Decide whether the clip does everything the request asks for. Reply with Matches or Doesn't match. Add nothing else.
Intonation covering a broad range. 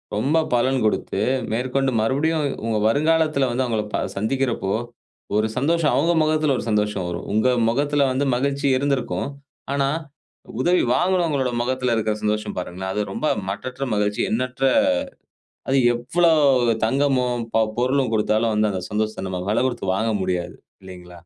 Doesn't match